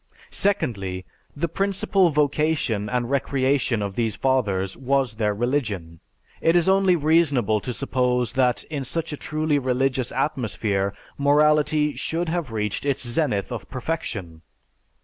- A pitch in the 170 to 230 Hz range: No, low, 130 Hz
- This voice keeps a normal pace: No, slow, 130 wpm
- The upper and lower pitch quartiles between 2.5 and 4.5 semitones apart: No, wide, 5.6 semitones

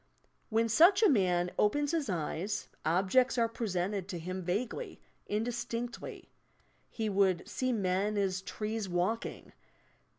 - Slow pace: Yes, slow, 125 wpm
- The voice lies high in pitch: Yes, high, 210 Hz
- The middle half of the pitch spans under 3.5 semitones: No, average, 4.2 semitones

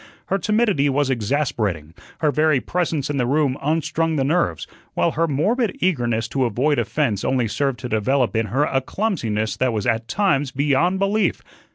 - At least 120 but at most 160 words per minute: No, average, 175 wpm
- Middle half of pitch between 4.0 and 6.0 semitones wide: Yes, average, 5.3 semitones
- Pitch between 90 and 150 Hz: Yes, medium, 140 Hz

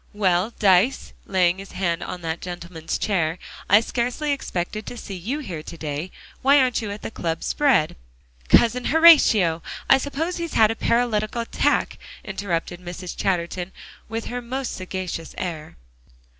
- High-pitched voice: Yes, high, 195 Hz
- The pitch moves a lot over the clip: Yes, wide, 5.7 semitones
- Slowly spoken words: No, average, 155 wpm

